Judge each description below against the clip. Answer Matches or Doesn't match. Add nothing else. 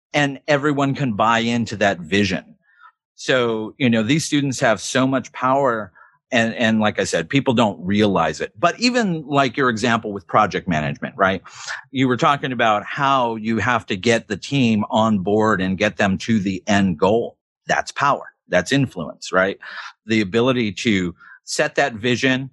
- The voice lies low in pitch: Matches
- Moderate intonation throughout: Matches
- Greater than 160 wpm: Matches